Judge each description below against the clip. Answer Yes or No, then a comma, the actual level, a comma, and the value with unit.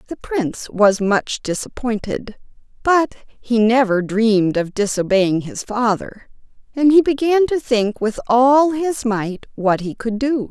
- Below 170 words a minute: Yes, average, 150 wpm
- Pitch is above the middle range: Yes, high, 235 Hz